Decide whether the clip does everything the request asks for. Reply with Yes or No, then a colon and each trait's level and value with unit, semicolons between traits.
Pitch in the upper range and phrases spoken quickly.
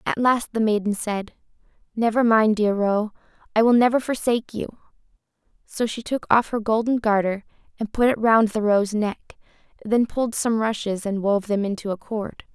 No: high, 220 Hz; average, 180 wpm